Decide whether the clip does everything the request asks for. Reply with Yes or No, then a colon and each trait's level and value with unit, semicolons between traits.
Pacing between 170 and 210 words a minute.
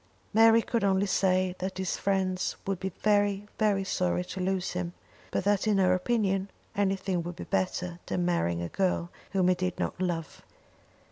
Yes: average, 180 wpm